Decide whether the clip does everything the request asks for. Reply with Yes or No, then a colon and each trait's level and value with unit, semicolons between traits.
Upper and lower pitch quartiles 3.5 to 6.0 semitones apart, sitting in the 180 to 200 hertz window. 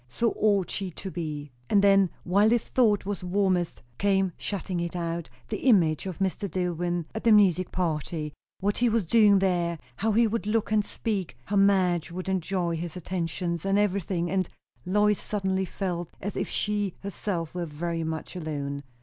No: average, 3.0 semitones; medium, 185 Hz